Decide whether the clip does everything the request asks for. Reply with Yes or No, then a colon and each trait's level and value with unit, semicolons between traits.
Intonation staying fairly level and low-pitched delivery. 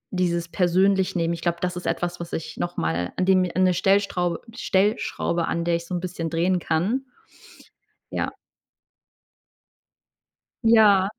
No: narrow, 1.9 semitones; medium, 180 Hz